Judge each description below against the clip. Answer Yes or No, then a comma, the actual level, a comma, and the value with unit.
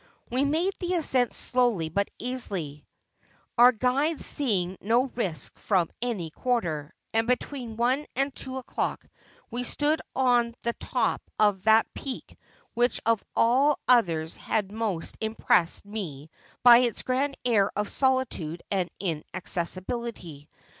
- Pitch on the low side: No, high, 230 Hz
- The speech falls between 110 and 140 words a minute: Yes, slow, 135 wpm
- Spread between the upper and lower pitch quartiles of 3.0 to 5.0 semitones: No, wide, 5.4 semitones